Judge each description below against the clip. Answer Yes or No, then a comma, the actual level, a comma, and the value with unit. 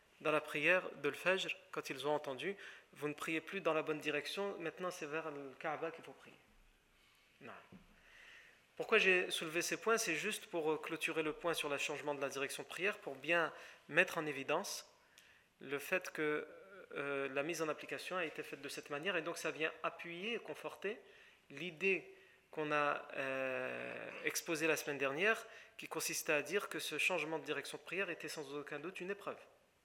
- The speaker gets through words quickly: No, average, 195 wpm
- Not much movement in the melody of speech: No, average, 3.7 semitones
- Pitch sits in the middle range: Yes, medium, 160 Hz